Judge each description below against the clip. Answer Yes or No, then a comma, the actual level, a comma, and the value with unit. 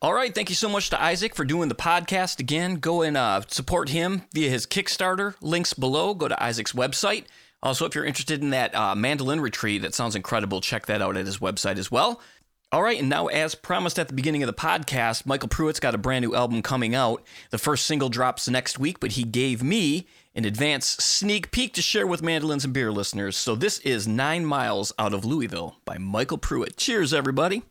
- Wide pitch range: Yes, wide, 6.4 semitones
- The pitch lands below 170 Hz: Yes, medium, 140 Hz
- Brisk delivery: Yes, fast, 220 wpm